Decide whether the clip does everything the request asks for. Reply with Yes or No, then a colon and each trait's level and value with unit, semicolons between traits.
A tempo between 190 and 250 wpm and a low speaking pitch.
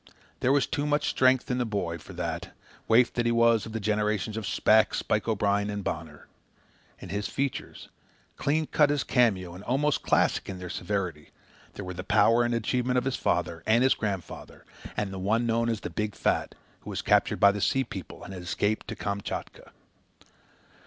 Yes: average, 195 wpm; low, 110 Hz